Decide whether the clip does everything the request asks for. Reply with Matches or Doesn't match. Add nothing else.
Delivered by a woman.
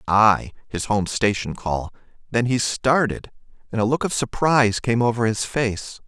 Doesn't match